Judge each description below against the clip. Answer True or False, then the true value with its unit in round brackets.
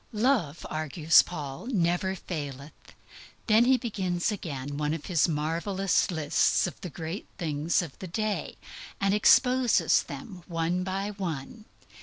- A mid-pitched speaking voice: True (175 Hz)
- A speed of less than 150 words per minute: True (140 wpm)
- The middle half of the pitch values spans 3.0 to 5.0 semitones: True (4.5 semitones)